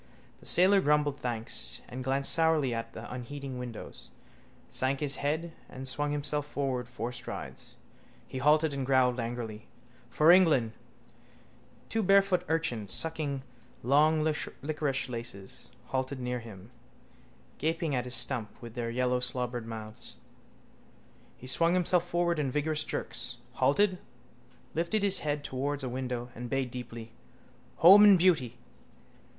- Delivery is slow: Yes, slow, 130 wpm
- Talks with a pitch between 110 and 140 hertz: Yes, low, 135 Hz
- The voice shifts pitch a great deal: No, average, 4.3 semitones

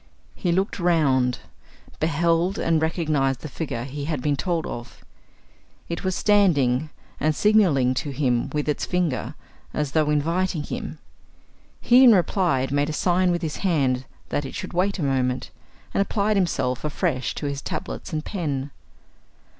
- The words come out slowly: No, average, 155 wpm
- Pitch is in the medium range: Yes, medium, 155 Hz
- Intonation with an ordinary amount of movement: Yes, average, 4.6 semitones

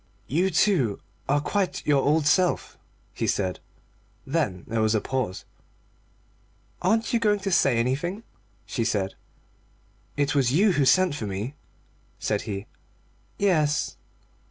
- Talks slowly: Yes, slow, 130 wpm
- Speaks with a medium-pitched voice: Yes, medium, 145 Hz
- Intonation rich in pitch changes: Yes, wide, 8.2 semitones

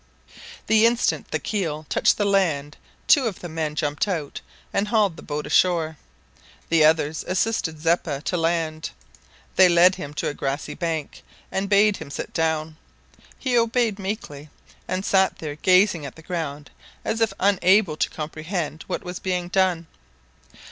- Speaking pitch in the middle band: Yes, medium, 170 Hz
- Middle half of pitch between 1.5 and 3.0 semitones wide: No, average, 4.0 semitones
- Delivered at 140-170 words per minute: Yes, average, 160 wpm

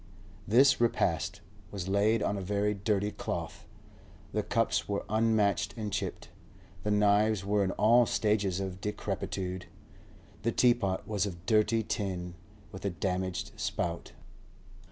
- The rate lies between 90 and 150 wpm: Yes, slow, 135 wpm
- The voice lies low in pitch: Yes, low, 100 Hz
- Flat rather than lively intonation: Yes, narrow, 2.2 semitones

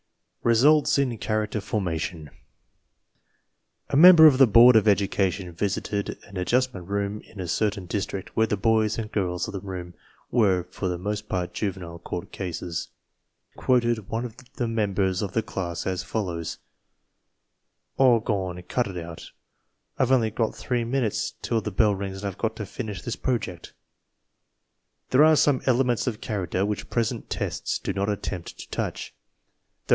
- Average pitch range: Yes, average, 3.9 semitones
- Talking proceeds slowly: No, average, 165 wpm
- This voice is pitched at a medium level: No, low, 105 Hz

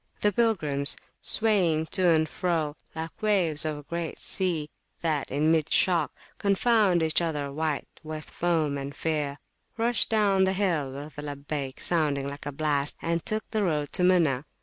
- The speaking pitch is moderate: Yes, medium, 160 Hz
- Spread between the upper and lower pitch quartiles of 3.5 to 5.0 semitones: Yes, average, 3.9 semitones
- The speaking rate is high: No, average, 170 wpm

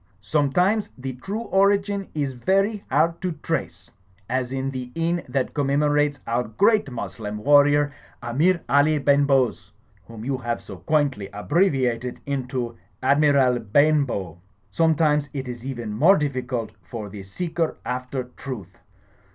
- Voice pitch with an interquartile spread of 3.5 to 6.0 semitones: Yes, average, 4.1 semitones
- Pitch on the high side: No, low, 135 Hz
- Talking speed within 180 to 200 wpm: No, slow, 135 wpm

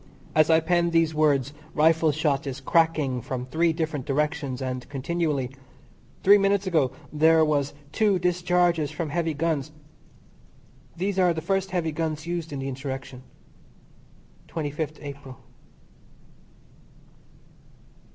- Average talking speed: No, slow, 125 wpm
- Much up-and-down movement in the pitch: No, average, 3.3 semitones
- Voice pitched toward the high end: No, medium, 155 Hz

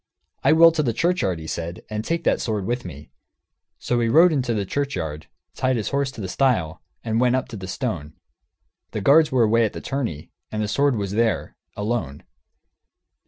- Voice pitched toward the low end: Yes, low, 115 Hz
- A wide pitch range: Yes, wide, 6.1 semitones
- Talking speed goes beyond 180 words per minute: Yes, average, 200 wpm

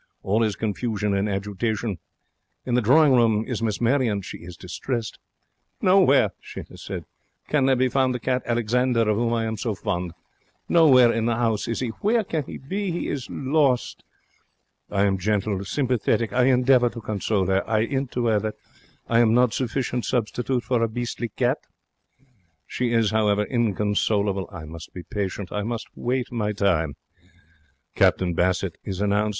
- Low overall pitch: Yes, low, 115 Hz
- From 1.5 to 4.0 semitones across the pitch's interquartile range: Yes, average, 3.5 semitones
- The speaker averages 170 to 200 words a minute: Yes, average, 175 wpm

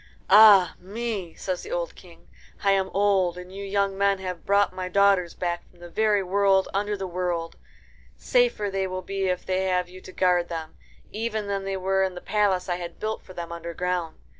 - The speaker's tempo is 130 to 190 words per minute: No, fast, 205 wpm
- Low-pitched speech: No, high, 190 Hz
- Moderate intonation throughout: No, narrow, 1.9 semitones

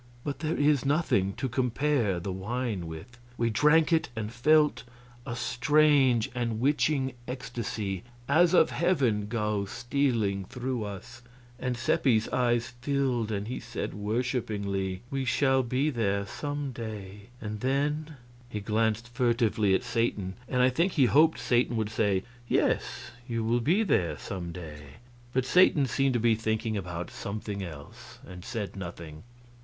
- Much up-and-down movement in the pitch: No, average, 4.5 semitones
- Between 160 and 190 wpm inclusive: No, average, 150 wpm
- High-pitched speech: No, low, 120 Hz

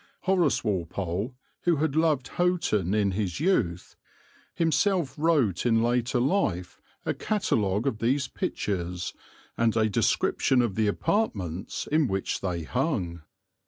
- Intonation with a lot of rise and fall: Yes, wide, 8.2 semitones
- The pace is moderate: No, slow, 125 wpm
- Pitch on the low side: Yes, low, 115 Hz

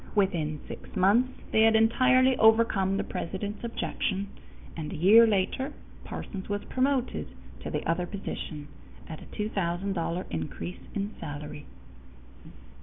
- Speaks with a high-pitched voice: Yes, high, 200 Hz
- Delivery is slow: Yes, slow, 125 wpm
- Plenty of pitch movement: No, average, 4.7 semitones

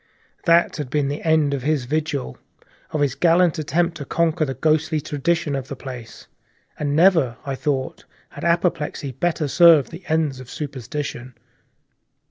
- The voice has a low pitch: No, medium, 150 Hz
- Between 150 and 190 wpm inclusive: Yes, average, 155 wpm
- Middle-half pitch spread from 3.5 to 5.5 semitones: No, average, 3.1 semitones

